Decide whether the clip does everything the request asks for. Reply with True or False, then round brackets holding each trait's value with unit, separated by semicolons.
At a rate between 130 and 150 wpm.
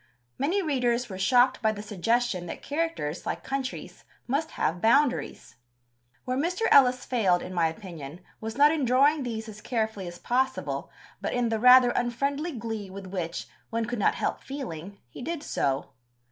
False (170 wpm)